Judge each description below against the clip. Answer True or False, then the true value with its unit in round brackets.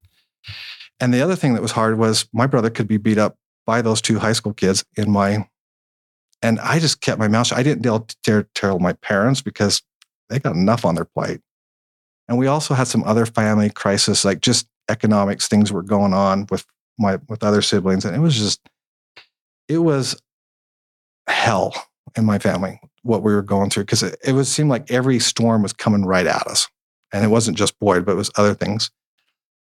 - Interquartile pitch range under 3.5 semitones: True (3.0 semitones)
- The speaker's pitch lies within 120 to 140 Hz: False (110 Hz)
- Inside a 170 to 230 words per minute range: True (205 wpm)